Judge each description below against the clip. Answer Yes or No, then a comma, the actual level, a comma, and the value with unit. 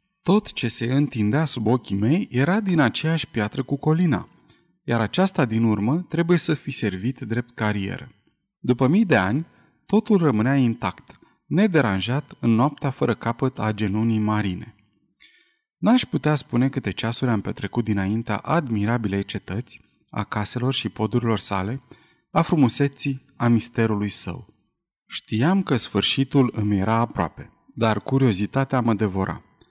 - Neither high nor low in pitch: No, low, 120 Hz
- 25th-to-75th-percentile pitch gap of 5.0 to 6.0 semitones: Yes, average, 5.3 semitones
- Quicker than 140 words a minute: No, average, 135 wpm